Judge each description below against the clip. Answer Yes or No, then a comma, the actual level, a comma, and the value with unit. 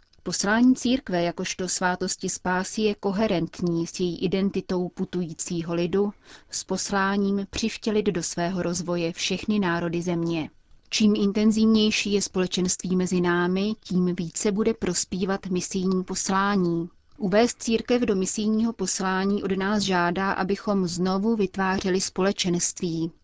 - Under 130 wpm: Yes, slow, 115 wpm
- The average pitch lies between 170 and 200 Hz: Yes, high, 190 Hz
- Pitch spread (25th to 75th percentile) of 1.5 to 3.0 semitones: Yes, narrow, 2.4 semitones